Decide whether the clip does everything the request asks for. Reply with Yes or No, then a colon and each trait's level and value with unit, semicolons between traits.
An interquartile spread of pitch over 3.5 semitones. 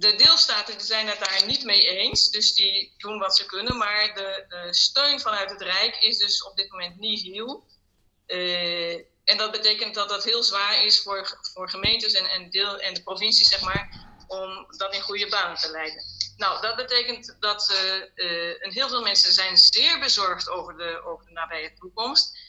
No: average, 2.8 semitones